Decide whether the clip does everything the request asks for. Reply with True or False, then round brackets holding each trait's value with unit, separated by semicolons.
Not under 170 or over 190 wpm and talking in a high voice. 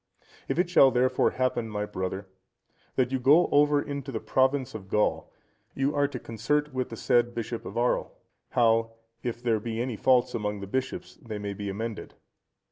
False (185 wpm; 120 Hz)